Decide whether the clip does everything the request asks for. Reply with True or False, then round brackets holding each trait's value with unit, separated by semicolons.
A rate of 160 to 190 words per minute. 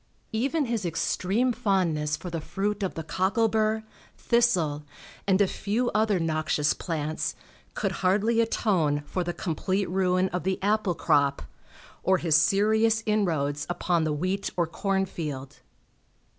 False (145 wpm)